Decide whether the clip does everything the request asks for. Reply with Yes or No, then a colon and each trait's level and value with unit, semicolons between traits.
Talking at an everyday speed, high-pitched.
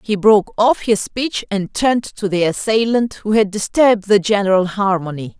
Yes: average, 180 wpm; high, 205 Hz